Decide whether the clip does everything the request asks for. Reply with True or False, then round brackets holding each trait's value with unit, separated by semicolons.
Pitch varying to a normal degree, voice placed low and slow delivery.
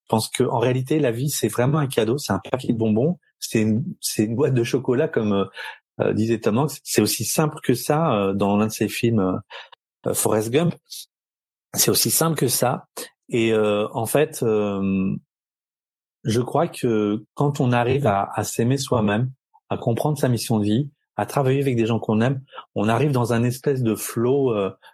False (4.5 semitones; 120 Hz; 200 wpm)